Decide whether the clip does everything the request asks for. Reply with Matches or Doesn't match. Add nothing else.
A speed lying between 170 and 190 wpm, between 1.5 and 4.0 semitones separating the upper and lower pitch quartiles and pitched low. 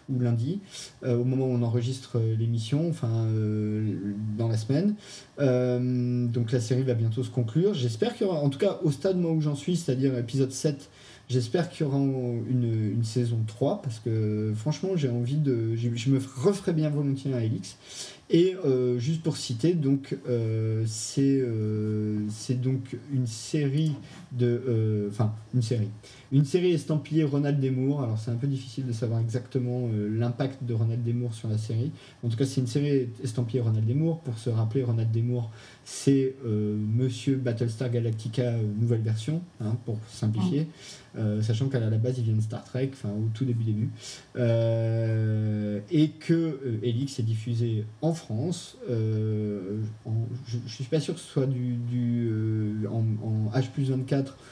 Matches